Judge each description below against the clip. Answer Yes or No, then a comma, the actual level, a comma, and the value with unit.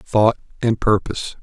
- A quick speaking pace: No, slow, 125 wpm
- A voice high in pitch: No, low, 110 Hz